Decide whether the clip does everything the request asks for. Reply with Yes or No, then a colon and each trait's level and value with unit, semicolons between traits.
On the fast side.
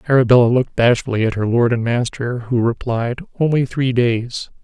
No: average, 170 wpm